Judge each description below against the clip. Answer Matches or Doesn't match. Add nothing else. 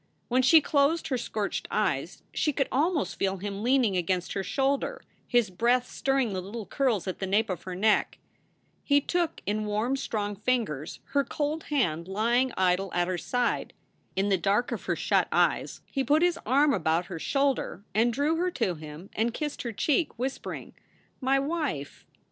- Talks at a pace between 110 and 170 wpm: Doesn't match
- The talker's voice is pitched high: Matches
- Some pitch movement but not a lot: Doesn't match